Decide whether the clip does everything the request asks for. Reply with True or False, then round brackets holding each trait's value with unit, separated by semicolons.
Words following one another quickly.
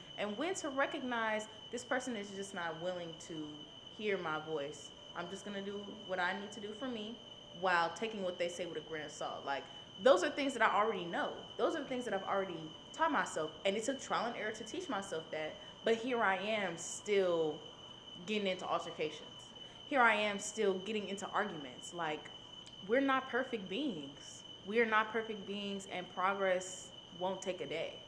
False (195 wpm)